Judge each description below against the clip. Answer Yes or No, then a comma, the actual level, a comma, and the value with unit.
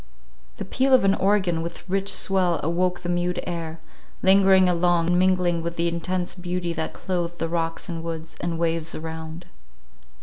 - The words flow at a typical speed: Yes, average, 170 wpm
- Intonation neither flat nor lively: No, narrow, 1.8 semitones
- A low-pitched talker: No, medium, 175 Hz